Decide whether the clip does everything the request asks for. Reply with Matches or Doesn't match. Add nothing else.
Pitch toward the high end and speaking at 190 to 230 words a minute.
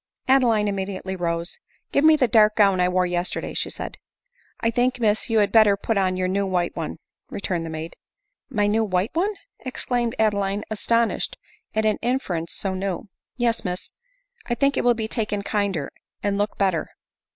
Matches